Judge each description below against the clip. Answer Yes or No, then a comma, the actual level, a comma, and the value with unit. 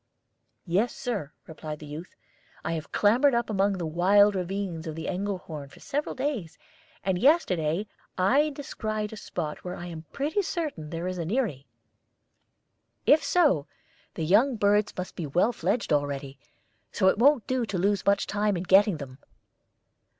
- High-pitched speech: Yes, high, 195 Hz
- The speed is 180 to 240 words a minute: No, average, 165 wpm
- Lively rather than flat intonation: Yes, wide, 5.7 semitones